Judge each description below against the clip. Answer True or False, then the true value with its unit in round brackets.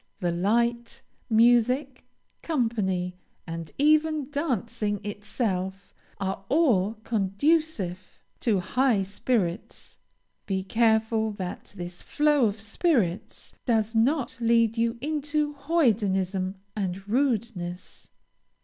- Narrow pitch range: False (5.2 semitones)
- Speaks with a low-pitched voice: False (225 Hz)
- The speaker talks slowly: True (95 wpm)